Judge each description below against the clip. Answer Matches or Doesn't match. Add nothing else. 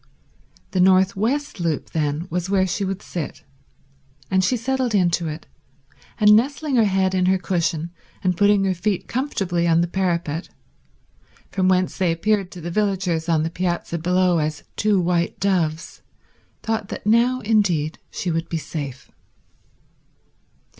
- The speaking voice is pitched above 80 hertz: Matches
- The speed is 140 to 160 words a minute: Matches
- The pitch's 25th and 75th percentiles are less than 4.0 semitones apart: Matches